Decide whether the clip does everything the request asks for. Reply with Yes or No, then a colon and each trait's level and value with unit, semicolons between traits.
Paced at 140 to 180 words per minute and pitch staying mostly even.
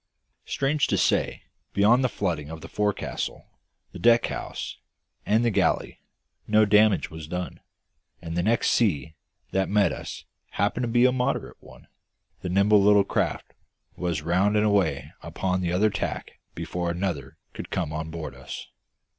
No: average, 160 wpm; average, 4.1 semitones